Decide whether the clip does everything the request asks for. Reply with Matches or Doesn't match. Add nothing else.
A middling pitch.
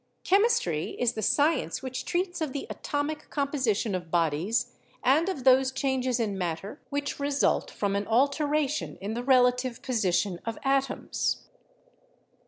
Doesn't match